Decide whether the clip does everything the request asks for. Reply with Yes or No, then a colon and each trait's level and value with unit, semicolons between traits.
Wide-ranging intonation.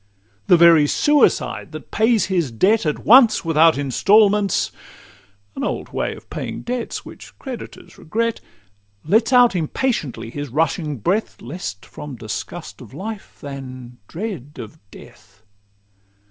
Yes: wide, 8.5 semitones